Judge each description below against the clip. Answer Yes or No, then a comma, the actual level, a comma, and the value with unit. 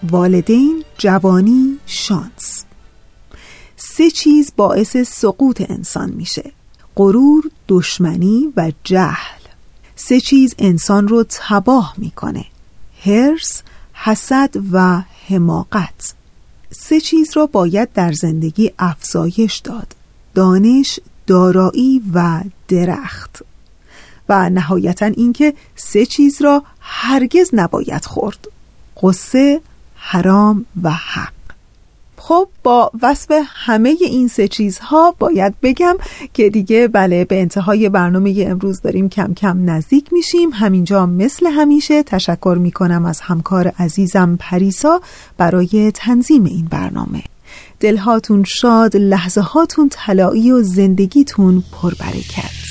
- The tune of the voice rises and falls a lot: Yes, wide, 6.4 semitones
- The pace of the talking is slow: Yes, slow, 100 wpm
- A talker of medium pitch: No, high, 205 Hz